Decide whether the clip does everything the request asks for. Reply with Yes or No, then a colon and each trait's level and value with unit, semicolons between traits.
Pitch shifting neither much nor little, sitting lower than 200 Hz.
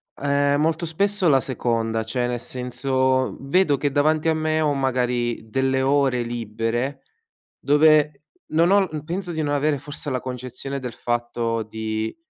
Yes: average, 4.0 semitones; low, 135 Hz